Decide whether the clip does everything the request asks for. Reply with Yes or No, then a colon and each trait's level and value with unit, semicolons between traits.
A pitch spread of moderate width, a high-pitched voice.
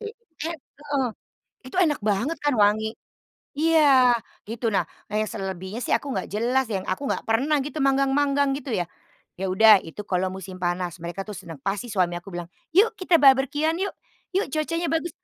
No: wide, 7.1 semitones; high, 240 Hz